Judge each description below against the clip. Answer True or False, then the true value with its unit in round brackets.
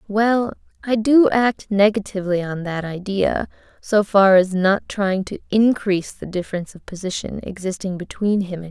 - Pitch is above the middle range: True (200 Hz)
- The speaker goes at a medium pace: True (165 wpm)